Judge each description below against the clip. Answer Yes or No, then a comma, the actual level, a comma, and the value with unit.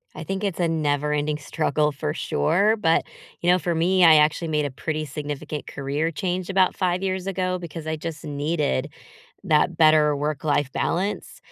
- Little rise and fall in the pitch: No, average, 3.1 semitones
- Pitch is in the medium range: Yes, medium, 155 Hz